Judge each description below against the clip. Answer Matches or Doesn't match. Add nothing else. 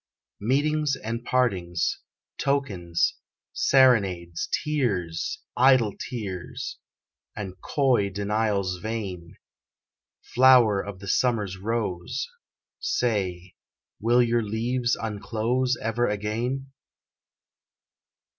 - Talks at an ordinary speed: Doesn't match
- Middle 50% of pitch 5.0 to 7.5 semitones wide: Doesn't match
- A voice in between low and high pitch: Doesn't match